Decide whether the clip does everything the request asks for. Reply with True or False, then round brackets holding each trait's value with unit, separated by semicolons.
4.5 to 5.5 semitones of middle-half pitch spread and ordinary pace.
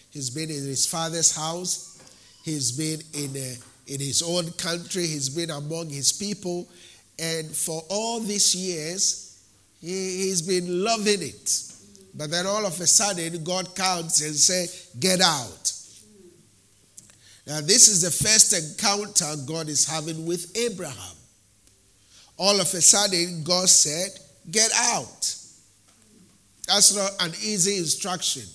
False (5.1 semitones; 130 wpm)